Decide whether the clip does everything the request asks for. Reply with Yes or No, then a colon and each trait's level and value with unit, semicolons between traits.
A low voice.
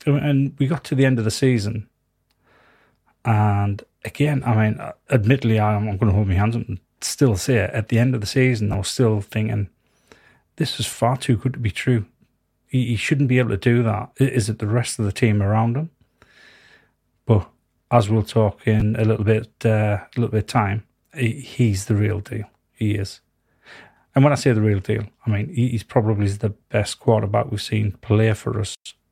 Yes: low, 110 Hz